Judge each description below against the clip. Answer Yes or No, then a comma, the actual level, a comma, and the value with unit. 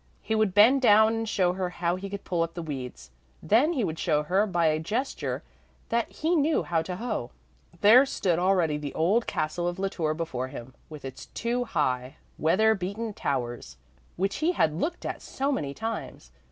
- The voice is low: No, medium, 185 Hz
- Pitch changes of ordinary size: No, wide, 6.2 semitones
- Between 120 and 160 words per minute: No, average, 195 wpm